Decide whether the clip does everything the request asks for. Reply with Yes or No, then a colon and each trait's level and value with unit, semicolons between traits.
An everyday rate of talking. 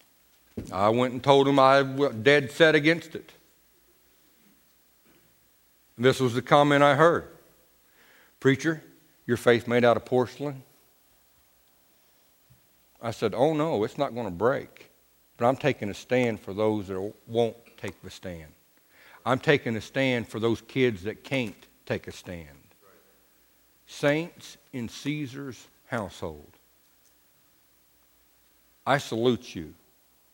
No: slow, 125 wpm